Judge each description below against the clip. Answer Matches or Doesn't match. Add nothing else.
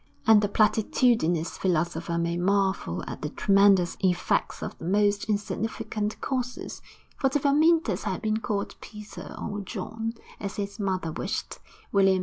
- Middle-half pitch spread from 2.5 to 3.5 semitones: Matches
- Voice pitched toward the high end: Matches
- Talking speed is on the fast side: Doesn't match